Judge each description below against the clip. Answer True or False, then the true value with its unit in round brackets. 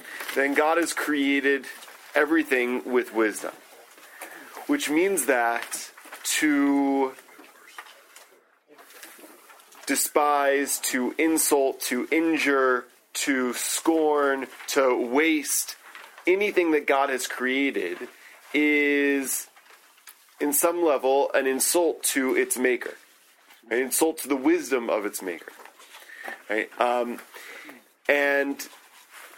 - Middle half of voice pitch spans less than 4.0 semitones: True (3.3 semitones)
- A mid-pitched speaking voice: True (145 Hz)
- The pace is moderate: False (95 wpm)